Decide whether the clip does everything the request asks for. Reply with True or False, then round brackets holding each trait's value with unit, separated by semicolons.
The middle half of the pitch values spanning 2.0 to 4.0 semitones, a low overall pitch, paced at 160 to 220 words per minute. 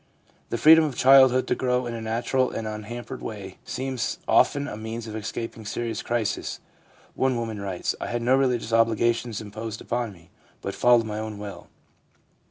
True (2.5 semitones; 115 Hz; 185 wpm)